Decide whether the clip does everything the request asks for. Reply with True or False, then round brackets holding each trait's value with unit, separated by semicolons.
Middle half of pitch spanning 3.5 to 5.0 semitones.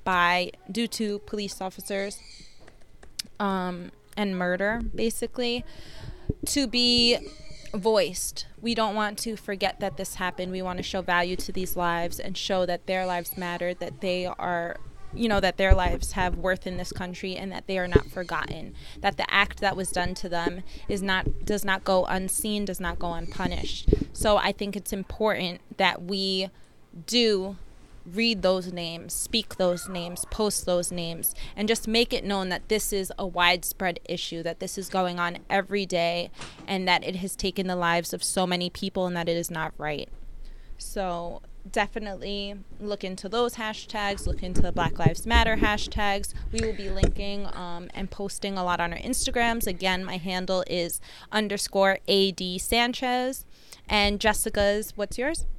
False (2.6 semitones)